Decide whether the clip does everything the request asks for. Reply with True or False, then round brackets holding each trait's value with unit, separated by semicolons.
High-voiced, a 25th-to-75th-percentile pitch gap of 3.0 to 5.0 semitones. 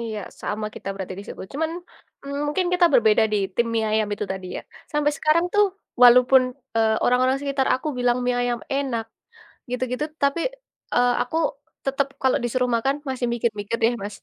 True (250 Hz; 3.7 semitones)